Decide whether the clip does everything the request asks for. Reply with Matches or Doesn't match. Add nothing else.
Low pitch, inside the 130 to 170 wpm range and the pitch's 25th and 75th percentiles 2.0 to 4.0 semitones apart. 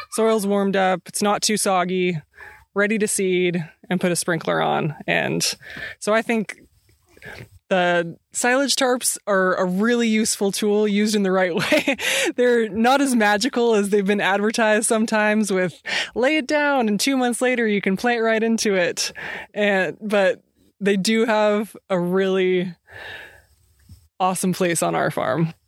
Doesn't match